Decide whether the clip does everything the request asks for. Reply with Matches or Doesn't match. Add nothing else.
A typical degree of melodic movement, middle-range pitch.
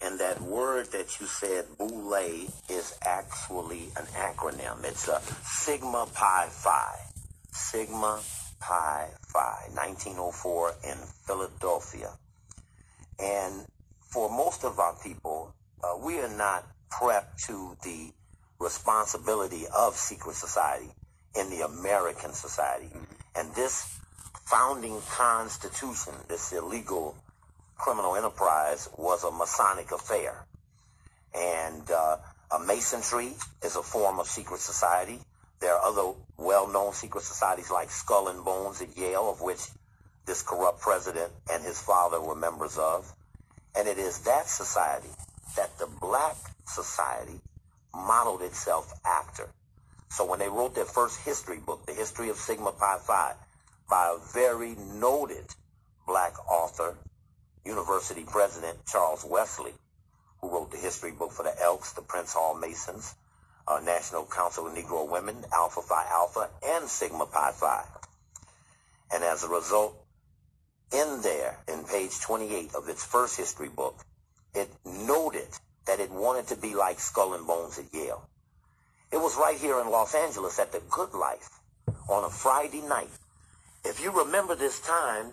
Doesn't match